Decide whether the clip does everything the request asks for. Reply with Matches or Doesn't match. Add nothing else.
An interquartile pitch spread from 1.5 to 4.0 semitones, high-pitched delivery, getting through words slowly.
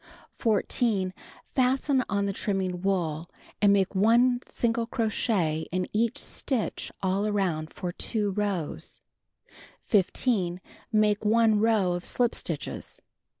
Matches